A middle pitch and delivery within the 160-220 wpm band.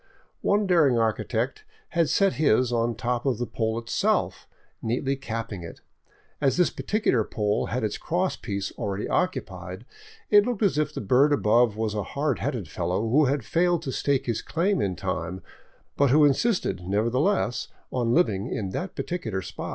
No: low, 125 Hz; average, 175 wpm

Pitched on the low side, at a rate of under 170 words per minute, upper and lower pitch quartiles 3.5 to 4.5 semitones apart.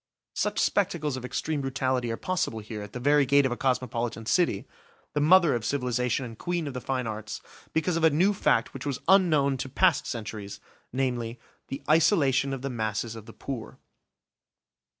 No: low, 130 Hz; average, 185 wpm; average, 4.2 semitones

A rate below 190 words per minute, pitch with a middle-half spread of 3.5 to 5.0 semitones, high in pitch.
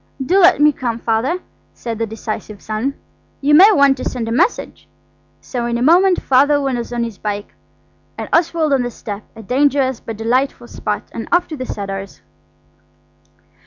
Yes: average, 165 wpm; average, 4.4 semitones; very high, 250 Hz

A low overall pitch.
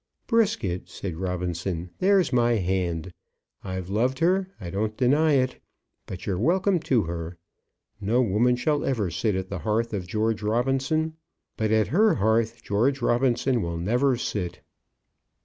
Yes: low, 110 Hz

